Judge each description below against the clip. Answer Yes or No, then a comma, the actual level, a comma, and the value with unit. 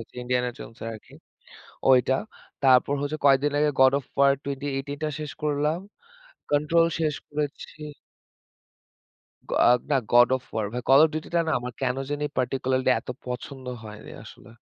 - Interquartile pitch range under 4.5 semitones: Yes, average, 2.8 semitones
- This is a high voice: No, low, 135 Hz